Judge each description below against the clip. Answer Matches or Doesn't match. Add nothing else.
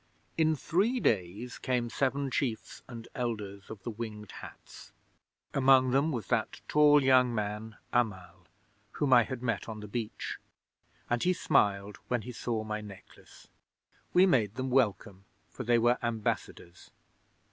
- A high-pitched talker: Doesn't match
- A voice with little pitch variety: Doesn't match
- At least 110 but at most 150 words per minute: Matches